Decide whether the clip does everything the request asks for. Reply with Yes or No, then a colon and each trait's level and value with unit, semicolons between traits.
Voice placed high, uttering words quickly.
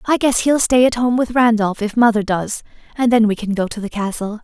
Yes: high, 225 Hz; fast, 255 wpm